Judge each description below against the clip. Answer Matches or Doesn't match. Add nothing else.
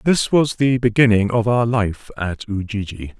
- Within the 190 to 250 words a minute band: Doesn't match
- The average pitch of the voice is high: Doesn't match